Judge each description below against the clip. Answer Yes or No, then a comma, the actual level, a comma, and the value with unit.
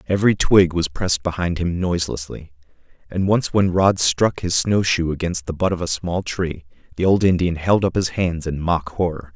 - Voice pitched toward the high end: No, very low, 85 Hz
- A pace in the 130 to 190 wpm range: No, fast, 205 wpm